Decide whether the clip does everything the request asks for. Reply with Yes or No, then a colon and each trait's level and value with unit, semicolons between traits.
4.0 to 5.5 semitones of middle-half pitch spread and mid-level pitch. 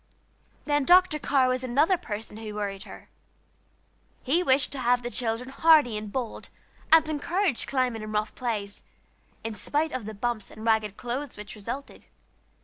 No: average, 4.8 semitones; high, 245 Hz